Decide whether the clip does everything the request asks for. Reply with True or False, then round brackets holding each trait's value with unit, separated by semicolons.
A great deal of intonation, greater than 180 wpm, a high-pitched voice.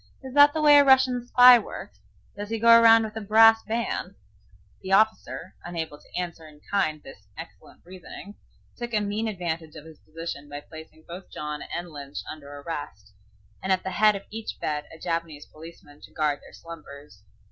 False (6.4 semitones; 190 wpm; 175 Hz)